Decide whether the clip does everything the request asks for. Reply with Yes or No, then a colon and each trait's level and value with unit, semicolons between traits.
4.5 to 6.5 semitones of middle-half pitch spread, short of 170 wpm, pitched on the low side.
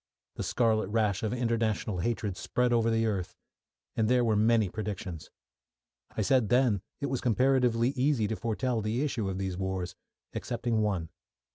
No: average, 3.1 semitones; average, 160 wpm; low, 110 Hz